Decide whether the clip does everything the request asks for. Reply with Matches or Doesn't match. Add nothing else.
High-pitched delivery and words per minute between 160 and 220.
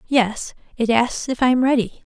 Matches